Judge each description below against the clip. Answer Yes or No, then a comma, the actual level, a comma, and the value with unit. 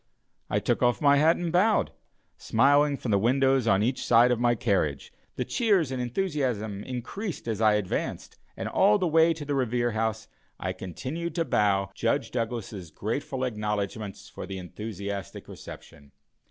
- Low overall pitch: Yes, low, 120 Hz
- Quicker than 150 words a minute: Yes, average, 165 wpm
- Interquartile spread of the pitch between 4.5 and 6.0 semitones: Yes, wide, 5.5 semitones